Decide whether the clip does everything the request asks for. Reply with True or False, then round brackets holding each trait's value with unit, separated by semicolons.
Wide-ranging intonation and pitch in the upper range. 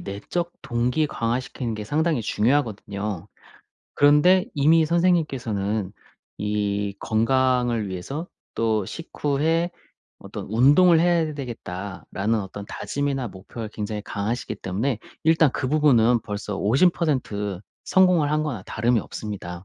False (6.5 semitones; 120 Hz)